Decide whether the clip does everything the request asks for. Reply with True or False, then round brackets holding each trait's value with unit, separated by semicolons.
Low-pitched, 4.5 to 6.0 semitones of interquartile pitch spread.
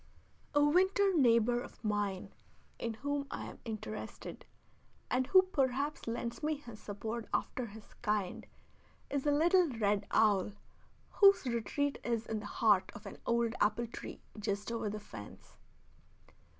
False (235 Hz; 5.3 semitones)